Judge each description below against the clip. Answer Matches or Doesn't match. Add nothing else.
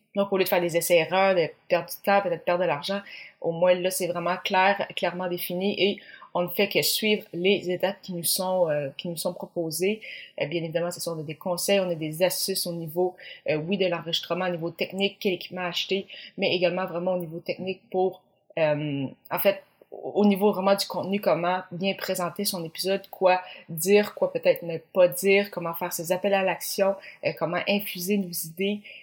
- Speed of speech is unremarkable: Matches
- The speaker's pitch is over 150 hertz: Matches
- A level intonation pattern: Matches